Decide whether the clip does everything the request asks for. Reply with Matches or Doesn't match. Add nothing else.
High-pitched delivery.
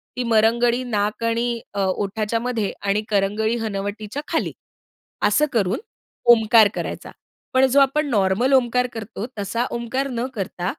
Matches